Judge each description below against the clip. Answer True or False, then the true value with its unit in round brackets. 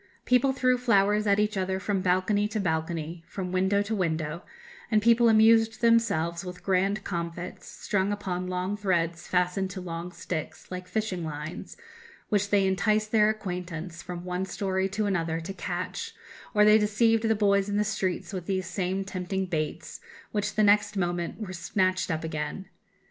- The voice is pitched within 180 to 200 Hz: True (190 Hz)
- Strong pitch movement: False (2.9 semitones)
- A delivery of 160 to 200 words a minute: True (170 wpm)